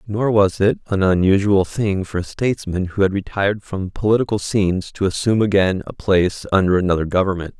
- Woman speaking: No, male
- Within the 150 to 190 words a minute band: Yes, average, 180 wpm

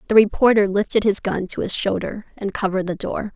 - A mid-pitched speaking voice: No, high, 205 Hz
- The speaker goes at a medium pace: No, fast, 215 wpm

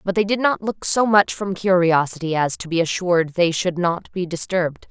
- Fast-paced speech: Yes, fast, 220 wpm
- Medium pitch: Yes, medium, 180 Hz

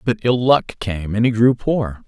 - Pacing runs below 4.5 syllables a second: Yes, 4.2 syllables/s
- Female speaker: No, male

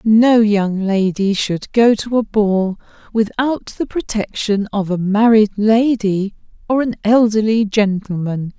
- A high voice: Yes, high, 210 Hz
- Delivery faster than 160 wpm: No, slow, 135 wpm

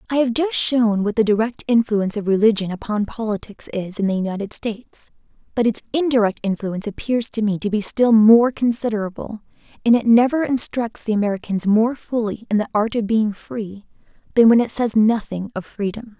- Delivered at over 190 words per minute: No, average, 185 wpm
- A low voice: No, high, 220 Hz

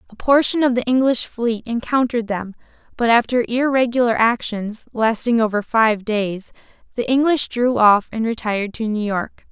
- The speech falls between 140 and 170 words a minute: Yes, average, 160 wpm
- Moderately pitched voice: No, high, 230 Hz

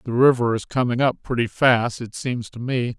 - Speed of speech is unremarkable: No, fast, 220 wpm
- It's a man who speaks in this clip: Yes, male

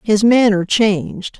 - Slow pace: Yes, slow, 130 wpm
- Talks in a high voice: Yes, high, 210 Hz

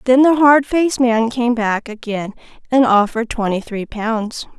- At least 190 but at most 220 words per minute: No, average, 170 wpm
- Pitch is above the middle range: Yes, high, 235 Hz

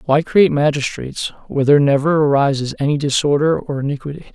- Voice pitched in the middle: Yes, medium, 145 Hz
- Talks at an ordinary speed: Yes, average, 150 wpm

